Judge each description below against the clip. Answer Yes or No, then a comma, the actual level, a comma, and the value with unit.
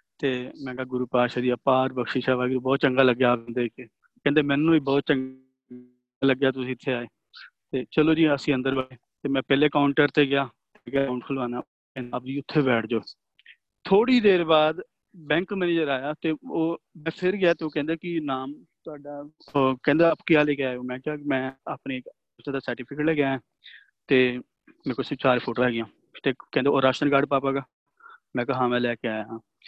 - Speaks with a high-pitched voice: No, low, 135 Hz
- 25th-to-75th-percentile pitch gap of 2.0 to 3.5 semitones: Yes, average, 2.9 semitones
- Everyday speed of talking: No, fast, 200 wpm